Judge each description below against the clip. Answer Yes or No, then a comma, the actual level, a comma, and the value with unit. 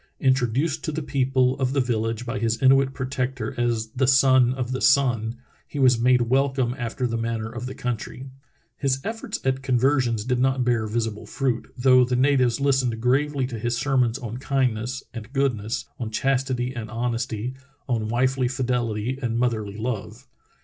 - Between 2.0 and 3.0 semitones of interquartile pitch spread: Yes, narrow, 2.4 semitones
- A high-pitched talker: No, low, 125 Hz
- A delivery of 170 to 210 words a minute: Yes, average, 175 wpm